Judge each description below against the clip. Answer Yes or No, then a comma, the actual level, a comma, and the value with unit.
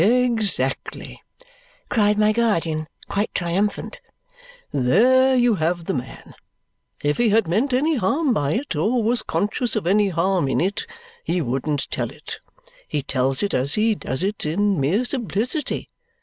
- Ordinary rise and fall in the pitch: No, wide, 7.0 semitones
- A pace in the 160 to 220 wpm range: No, average, 150 wpm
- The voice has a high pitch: Yes, high, 205 Hz